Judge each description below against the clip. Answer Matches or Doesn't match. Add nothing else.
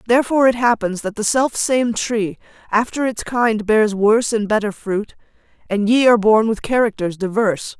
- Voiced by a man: Doesn't match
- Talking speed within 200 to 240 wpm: Doesn't match